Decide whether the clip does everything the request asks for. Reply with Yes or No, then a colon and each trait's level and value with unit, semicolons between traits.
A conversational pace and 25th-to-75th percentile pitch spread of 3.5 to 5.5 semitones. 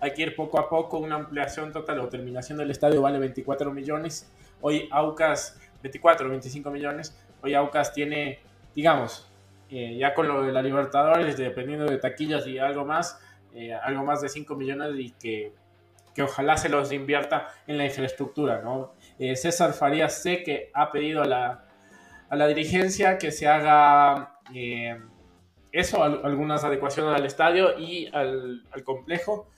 No: average, 165 wpm; narrow, 2.4 semitones